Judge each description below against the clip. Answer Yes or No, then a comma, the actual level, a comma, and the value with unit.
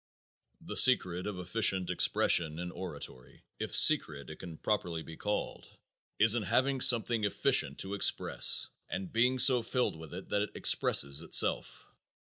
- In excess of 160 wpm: No, average, 155 wpm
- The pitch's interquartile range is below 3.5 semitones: No, wide, 5.5 semitones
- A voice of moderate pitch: No, very low, 95 Hz